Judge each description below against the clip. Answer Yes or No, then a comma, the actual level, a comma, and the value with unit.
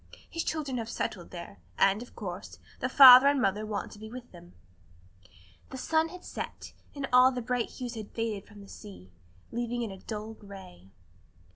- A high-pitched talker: Yes, high, 225 Hz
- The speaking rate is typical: Yes, average, 185 wpm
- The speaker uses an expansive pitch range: No, average, 4.1 semitones